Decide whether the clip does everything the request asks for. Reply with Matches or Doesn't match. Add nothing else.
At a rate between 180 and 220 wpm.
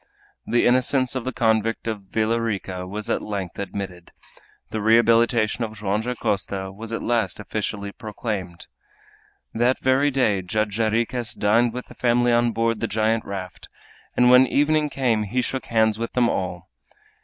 Doesn't match